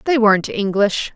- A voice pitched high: Yes, high, 215 Hz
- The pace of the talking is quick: No, average, 155 wpm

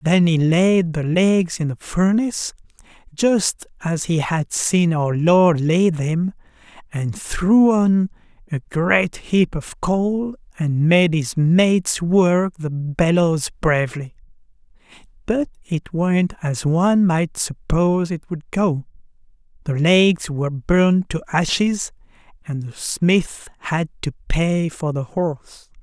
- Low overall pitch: No, medium, 170 Hz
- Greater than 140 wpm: No, slow, 135 wpm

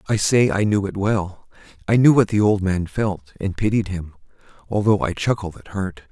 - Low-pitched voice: Yes, low, 100 Hz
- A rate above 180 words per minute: Yes, fast, 205 wpm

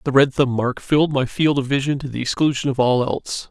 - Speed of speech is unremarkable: No, fast, 255 wpm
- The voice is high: No, low, 135 Hz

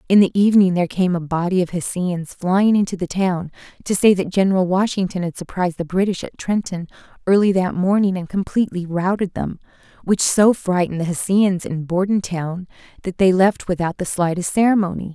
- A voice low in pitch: No, medium, 185 Hz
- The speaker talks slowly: No, average, 180 wpm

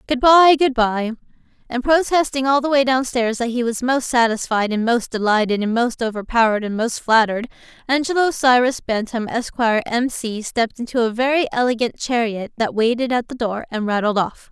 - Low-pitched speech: No, high, 240 Hz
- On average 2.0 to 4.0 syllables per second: No, 5.4 syllables/s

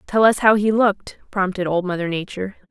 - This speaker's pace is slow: No, average, 200 wpm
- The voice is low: No, high, 195 Hz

